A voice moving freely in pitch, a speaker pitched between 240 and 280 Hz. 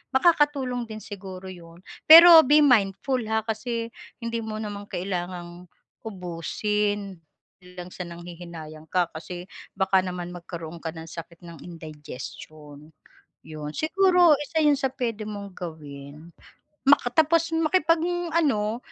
No: wide, 7.5 semitones; high, 200 Hz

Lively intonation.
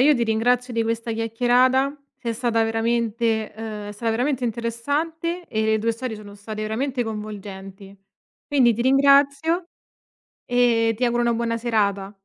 No: narrow, 2.4 semitones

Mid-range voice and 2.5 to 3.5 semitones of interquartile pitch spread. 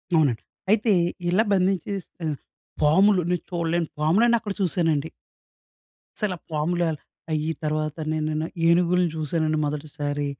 Yes: medium, 165 Hz; average, 3.1 semitones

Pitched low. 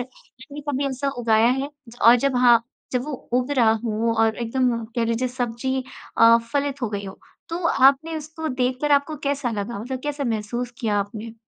No: very high, 250 Hz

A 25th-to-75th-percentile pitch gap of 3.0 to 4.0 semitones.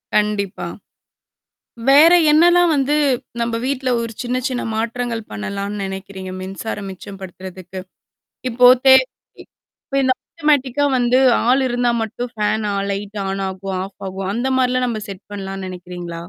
No: average, 4.7 semitones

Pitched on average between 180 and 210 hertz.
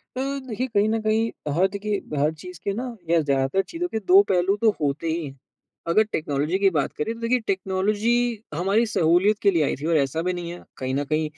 Yes: medium, 185 Hz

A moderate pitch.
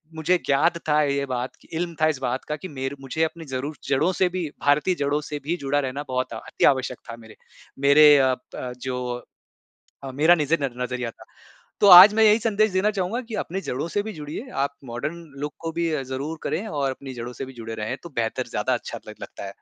Yes: medium, 145 Hz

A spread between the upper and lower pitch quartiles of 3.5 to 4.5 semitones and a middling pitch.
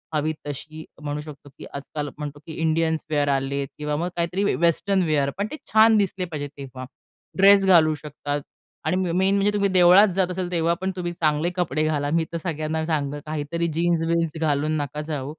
No: average, 3.1 semitones; medium, 160 Hz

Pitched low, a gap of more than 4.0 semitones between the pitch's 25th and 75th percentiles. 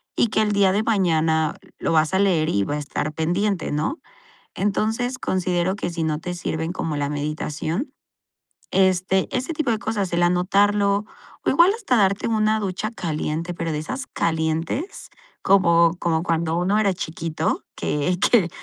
No: medium, 180 Hz; average, 4.4 semitones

